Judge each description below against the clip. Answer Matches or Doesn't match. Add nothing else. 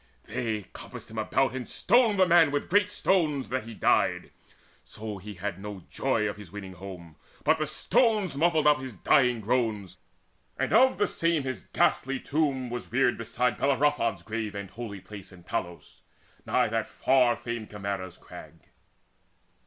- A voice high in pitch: Doesn't match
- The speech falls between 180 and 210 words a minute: Doesn't match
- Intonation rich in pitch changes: Matches